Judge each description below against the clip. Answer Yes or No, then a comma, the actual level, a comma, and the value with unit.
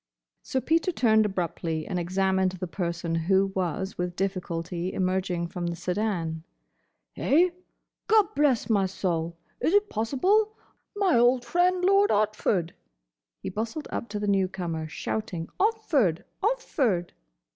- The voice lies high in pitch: Yes, high, 195 Hz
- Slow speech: Yes, slow, 120 wpm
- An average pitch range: No, wide, 8.2 semitones